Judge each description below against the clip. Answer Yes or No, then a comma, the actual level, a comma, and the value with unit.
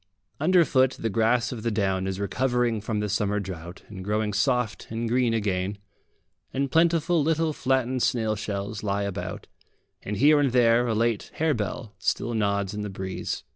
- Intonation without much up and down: No, average, 4.0 semitones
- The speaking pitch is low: Yes, low, 110 Hz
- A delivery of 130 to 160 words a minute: No, average, 170 wpm